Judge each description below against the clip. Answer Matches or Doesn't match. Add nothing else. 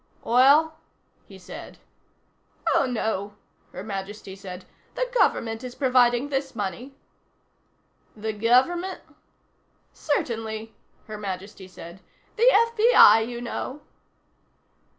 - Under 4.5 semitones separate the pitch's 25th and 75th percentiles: Doesn't match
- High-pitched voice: Matches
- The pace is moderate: Doesn't match